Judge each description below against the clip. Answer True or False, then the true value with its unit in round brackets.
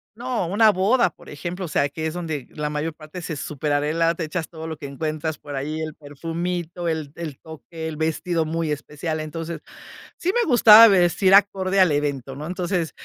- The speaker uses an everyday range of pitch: True (3.0 semitones)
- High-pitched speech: False (160 Hz)